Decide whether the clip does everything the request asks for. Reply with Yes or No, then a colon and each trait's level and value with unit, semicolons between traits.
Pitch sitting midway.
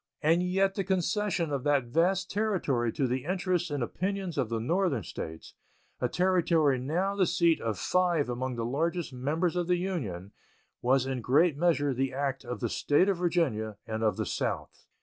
Yes: medium, 155 Hz